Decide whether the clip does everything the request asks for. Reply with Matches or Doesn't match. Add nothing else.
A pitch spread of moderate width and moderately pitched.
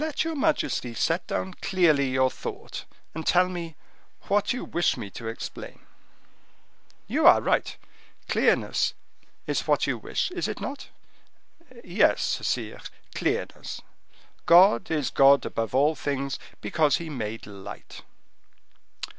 Doesn't match